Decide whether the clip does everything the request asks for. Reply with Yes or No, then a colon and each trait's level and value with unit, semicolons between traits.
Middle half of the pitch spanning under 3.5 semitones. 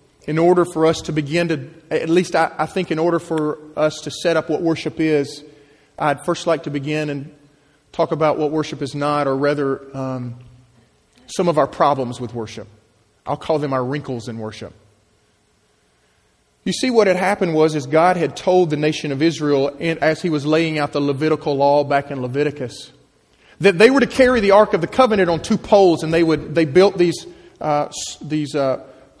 Yes: average, 2.8 semitones